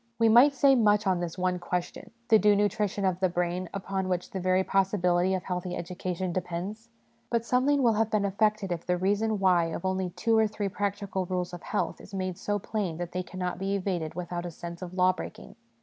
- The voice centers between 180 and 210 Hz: Yes, high, 190 Hz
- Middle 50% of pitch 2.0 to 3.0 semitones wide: Yes, narrow, 2.6 semitones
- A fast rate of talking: Yes, fast, 215 wpm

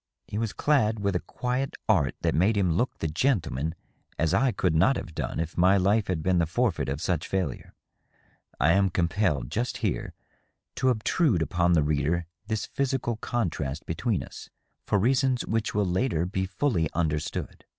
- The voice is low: Yes, very low, 95 Hz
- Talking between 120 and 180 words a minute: Yes, average, 175 wpm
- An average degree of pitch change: No, wide, 5.8 semitones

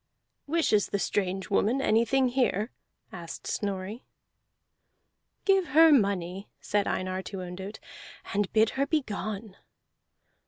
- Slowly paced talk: Yes, slow, 110 wpm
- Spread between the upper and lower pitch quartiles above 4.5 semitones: Yes, average, 5.3 semitones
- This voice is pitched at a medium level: No, high, 210 Hz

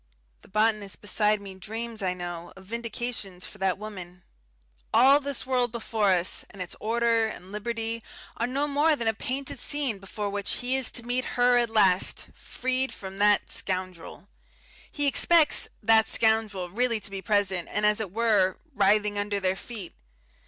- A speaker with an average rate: Yes, average, 170 wpm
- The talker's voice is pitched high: Yes, high, 215 Hz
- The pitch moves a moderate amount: Yes, average, 3.6 semitones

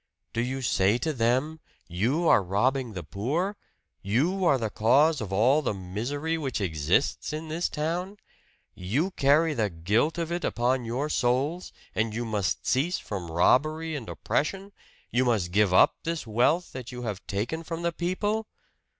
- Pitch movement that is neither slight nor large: No, wide, 7.1 semitones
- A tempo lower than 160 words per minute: No, average, 165 wpm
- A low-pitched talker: Yes, low, 130 Hz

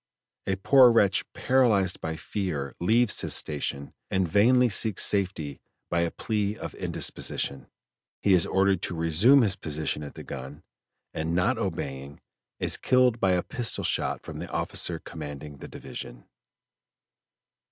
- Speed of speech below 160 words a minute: Yes, average, 145 wpm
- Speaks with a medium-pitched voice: No, very low, 95 Hz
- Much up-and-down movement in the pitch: Yes, wide, 6.1 semitones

